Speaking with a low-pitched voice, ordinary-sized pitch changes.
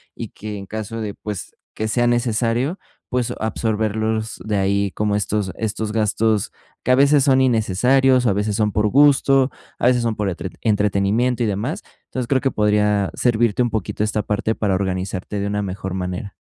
Yes: low, 110 Hz; average, 3.0 semitones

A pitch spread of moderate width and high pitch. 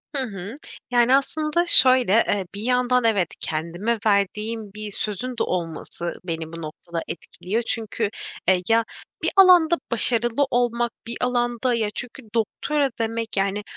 Yes: average, 4.0 semitones; high, 225 Hz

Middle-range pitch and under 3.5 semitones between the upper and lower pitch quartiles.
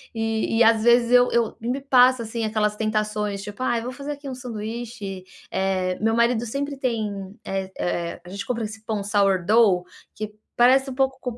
No: high, 225 Hz; average, 3.0 semitones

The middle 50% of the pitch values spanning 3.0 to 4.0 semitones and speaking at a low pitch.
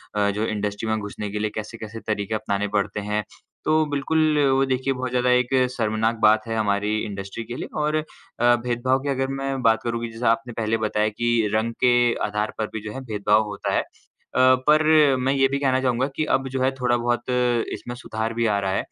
Yes: average, 3.5 semitones; low, 115 Hz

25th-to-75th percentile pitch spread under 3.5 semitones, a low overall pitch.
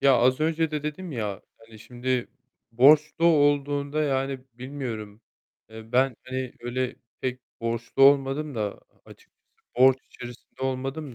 Yes: average, 3.0 semitones; low, 130 Hz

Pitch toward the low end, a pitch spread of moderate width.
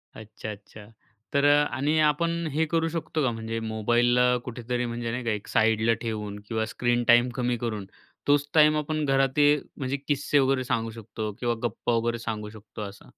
Yes: low, 120 Hz; average, 3.9 semitones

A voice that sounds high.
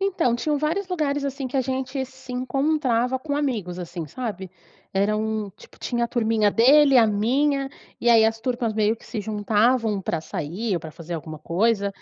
Yes: high, 235 Hz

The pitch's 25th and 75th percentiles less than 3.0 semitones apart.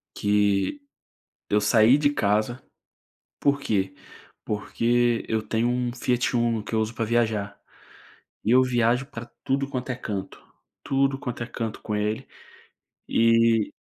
Yes: narrow, 2.6 semitones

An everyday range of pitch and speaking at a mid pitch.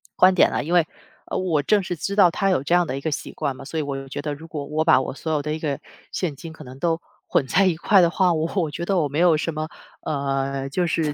Yes: average, 3.6 semitones; medium, 155 Hz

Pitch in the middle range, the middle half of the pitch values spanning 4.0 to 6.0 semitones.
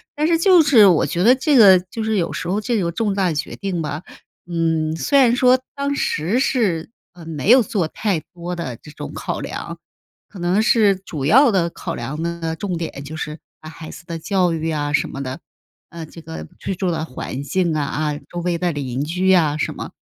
Yes: medium, 175 Hz; average, 5.1 semitones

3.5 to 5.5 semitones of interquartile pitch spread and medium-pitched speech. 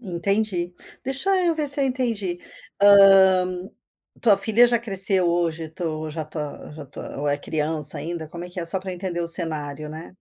Yes: average, 4.2 semitones; medium, 175 Hz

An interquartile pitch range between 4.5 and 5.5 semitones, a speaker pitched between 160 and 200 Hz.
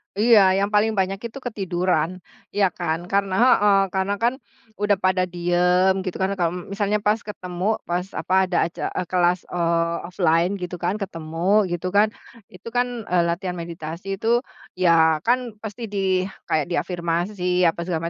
No: average, 2.8 semitones; medium, 185 Hz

